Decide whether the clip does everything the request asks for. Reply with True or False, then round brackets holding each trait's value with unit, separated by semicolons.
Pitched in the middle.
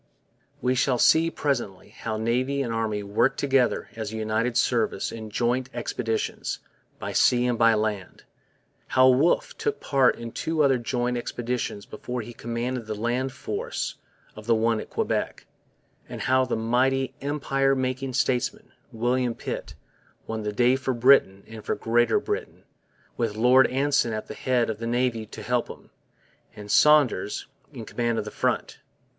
False (120 Hz)